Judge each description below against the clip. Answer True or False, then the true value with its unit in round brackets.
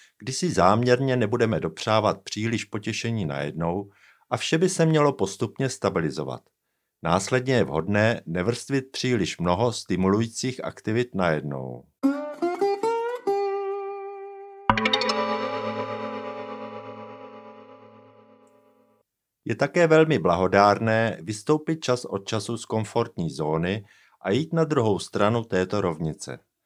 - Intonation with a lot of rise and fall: True (7.5 semitones)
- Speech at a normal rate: False (95 wpm)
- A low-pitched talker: True (115 Hz)